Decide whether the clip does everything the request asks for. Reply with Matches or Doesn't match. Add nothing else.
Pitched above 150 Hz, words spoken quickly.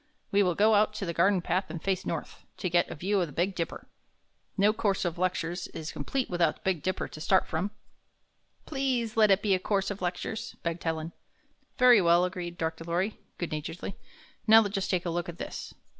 Matches